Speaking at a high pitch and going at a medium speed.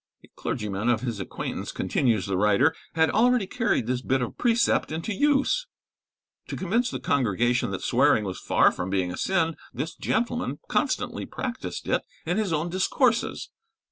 No: medium, 160 Hz; average, 165 wpm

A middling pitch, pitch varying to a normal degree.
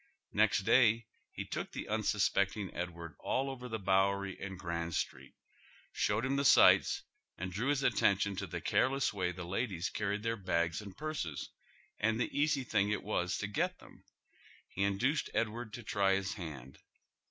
No: low, 100 Hz; average, 3.7 semitones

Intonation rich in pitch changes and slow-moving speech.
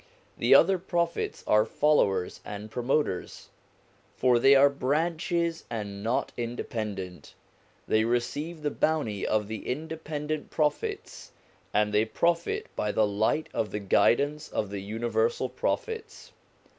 Yes: wide, 6.7 semitones; slow, 125 wpm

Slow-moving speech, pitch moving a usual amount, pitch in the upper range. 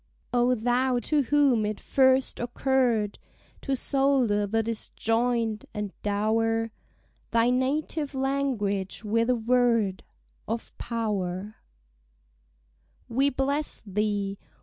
Yes: slow, 100 wpm; average, 3.7 semitones; high, 230 Hz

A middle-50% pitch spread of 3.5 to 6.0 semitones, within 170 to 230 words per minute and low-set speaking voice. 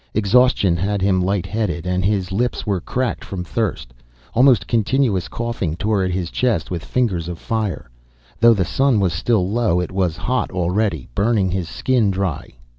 Yes: average, 4.2 semitones; average, 175 wpm; low, 100 Hz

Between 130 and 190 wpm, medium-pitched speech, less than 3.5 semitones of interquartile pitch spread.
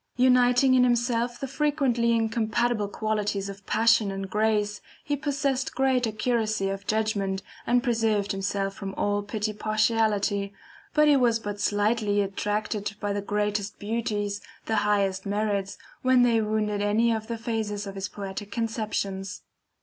No: average, 145 wpm; high, 215 Hz; narrow, 2.5 semitones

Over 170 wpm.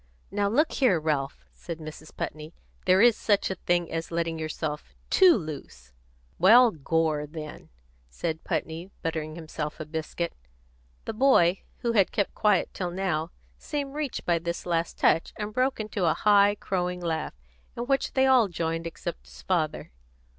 No: average, 160 wpm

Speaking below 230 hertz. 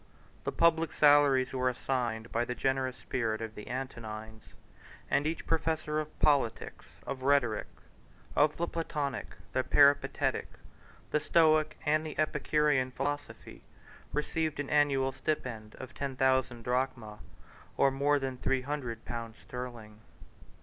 Yes: low, 135 Hz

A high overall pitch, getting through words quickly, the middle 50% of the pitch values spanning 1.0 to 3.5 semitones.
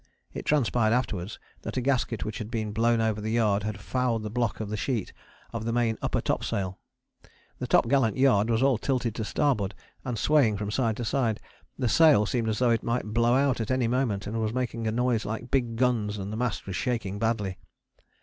No: low, 115 Hz; fast, 215 wpm; narrow, 2.6 semitones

